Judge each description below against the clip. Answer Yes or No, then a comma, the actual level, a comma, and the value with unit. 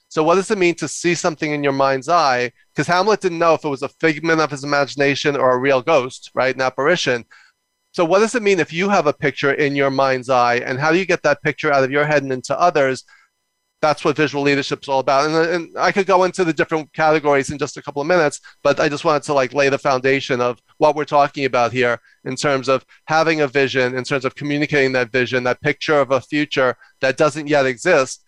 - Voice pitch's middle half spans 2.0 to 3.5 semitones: Yes, average, 2.9 semitones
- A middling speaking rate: No, fast, 250 wpm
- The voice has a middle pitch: Yes, medium, 145 Hz